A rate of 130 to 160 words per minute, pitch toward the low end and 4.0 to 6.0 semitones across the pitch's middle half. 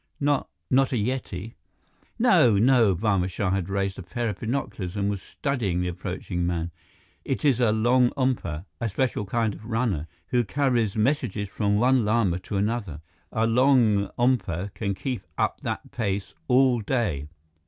Yes: average, 155 wpm; low, 110 Hz; average, 4.4 semitones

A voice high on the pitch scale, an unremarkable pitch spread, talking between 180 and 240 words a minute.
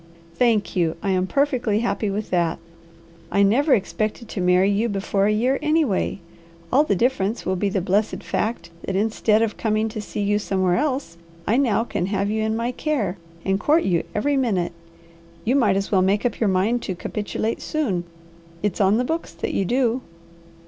Yes: high, 210 Hz; average, 3.8 semitones; average, 190 wpm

